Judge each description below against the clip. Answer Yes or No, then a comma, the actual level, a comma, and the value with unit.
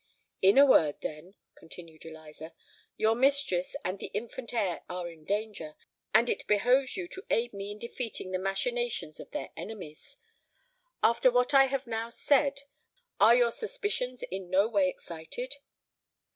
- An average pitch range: No, wide, 6.0 semitones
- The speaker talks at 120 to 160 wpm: Yes, average, 155 wpm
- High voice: Yes, high, 220 Hz